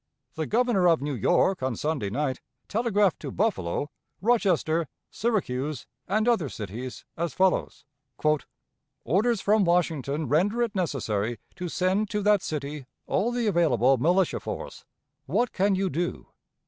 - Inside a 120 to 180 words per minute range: Yes, slow, 135 wpm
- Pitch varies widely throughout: Yes, wide, 6.6 semitones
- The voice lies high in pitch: No, medium, 175 Hz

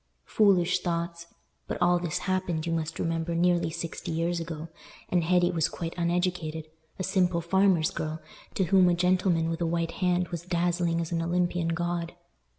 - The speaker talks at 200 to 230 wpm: No, average, 165 wpm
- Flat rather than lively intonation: Yes, narrow, 1.3 semitones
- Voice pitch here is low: No, medium, 170 Hz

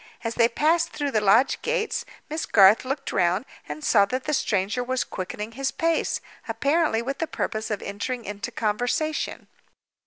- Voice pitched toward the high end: Yes, high, 245 Hz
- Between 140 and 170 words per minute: Yes, average, 165 wpm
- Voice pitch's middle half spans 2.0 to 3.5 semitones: No, wide, 5.6 semitones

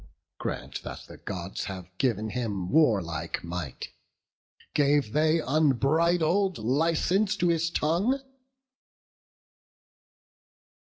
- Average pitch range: No, wide, 8.6 semitones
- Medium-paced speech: No, slow, 90 wpm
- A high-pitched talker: No, medium, 145 Hz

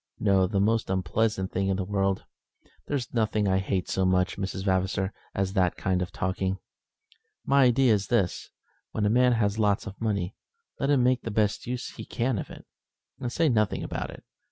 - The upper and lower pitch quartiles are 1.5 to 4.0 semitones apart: Yes, average, 3.3 semitones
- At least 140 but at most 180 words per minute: No, average, 195 wpm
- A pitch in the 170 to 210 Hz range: No, low, 100 Hz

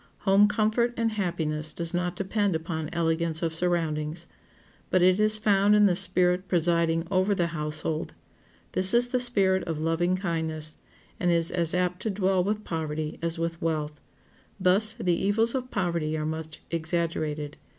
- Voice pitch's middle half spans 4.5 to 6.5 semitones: No, average, 3.4 semitones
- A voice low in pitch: No, medium, 175 Hz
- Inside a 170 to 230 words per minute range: No, average, 160 wpm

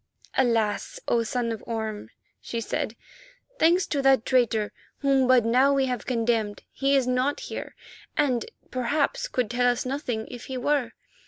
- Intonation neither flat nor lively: Yes, average, 3.0 semitones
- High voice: Yes, very high, 250 Hz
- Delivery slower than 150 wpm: No, average, 160 wpm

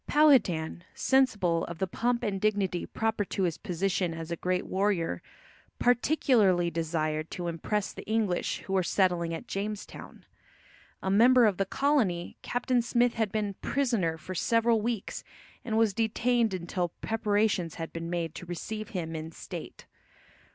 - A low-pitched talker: No, high, 195 Hz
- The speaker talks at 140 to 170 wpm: Yes, average, 150 wpm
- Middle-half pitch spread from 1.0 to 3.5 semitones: No, average, 4.7 semitones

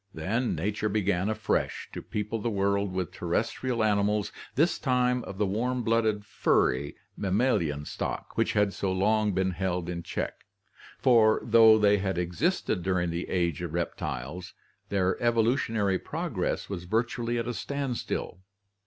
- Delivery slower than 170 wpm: Yes, average, 150 wpm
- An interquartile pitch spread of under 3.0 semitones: No, average, 3.9 semitones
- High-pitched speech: No, low, 105 Hz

